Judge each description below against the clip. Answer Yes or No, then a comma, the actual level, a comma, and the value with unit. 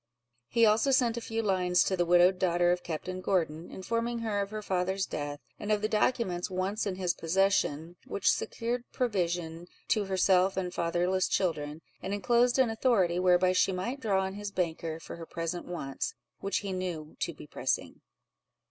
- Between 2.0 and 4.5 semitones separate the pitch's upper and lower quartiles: Yes, average, 3.2 semitones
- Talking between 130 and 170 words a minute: No, average, 180 wpm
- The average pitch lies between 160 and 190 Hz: Yes, medium, 185 Hz